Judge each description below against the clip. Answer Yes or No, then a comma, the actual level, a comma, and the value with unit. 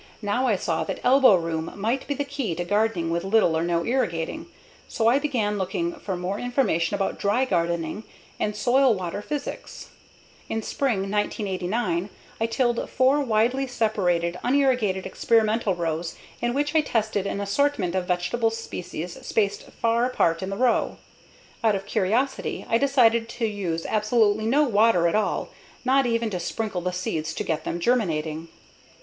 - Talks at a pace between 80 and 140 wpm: No, average, 160 wpm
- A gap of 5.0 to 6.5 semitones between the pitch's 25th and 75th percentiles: Yes, wide, 5.4 semitones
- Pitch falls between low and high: No, high, 210 Hz